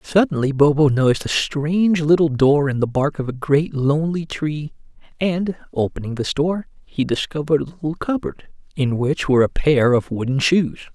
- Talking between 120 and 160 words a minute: No, average, 175 wpm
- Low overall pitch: No, medium, 150 Hz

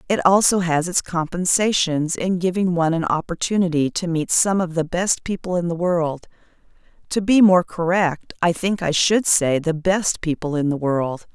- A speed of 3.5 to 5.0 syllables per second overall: Yes, 4.7 syllables/s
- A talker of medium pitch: Yes, medium, 175 Hz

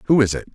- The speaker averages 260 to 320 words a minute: No, fast, 330 wpm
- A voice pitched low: Yes, low, 115 Hz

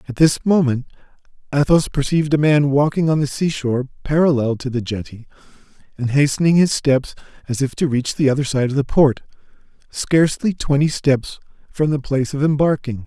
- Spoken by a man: Yes, male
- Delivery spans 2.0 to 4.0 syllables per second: No, 5.6 syllables/s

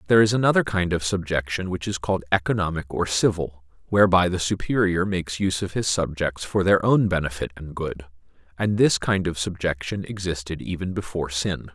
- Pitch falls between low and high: No, very low, 90 Hz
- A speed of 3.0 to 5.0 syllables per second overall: No, 5.7 syllables/s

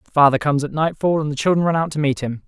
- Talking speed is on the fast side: Yes, fast, 315 wpm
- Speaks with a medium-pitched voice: Yes, medium, 150 Hz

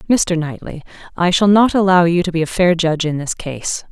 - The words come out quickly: Yes, fast, 230 wpm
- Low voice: No, medium, 175 Hz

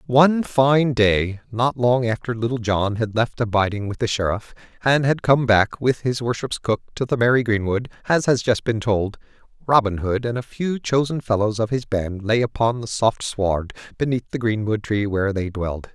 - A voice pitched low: Yes, low, 115 Hz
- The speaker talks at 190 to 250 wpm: Yes, average, 200 wpm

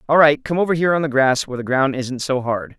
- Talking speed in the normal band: No, fast, 300 wpm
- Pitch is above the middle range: No, medium, 140 Hz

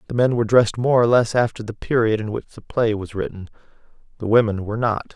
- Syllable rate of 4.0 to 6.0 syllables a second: No, 6.6 syllables/s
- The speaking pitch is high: No, low, 110 Hz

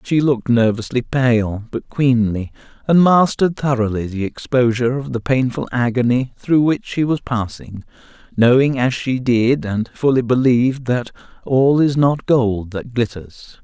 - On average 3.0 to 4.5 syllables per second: Yes, 4.4 syllables/s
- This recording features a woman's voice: No, male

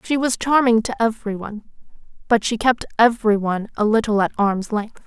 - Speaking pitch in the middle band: No, high, 220 Hz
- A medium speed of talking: Yes, average, 190 wpm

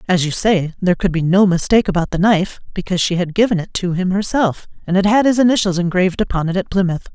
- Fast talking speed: Yes, fast, 245 wpm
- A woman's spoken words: Yes, female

